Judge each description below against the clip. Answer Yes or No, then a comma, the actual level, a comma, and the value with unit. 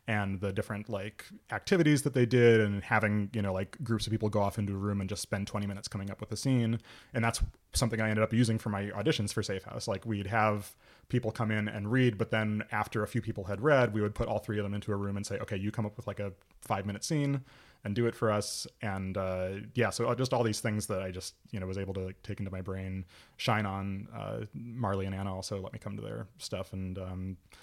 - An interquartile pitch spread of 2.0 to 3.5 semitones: Yes, narrow, 2.5 semitones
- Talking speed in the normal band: No, fast, 265 wpm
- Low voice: Yes, low, 105 Hz